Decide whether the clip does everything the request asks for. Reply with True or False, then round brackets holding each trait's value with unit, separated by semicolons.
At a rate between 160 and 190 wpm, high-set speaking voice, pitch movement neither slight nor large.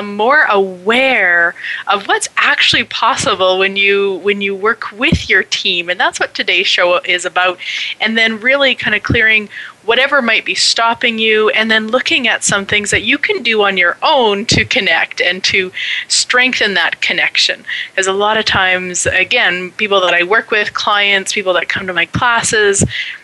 True (180 wpm; 205 Hz; 3.6 semitones)